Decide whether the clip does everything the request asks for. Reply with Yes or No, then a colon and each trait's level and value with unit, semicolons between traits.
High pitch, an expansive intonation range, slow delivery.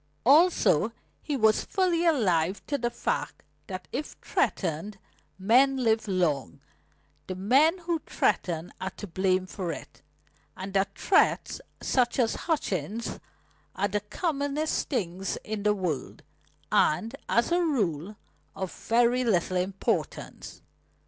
Yes: high, 210 Hz; wide, 6.8 semitones; slow, 125 wpm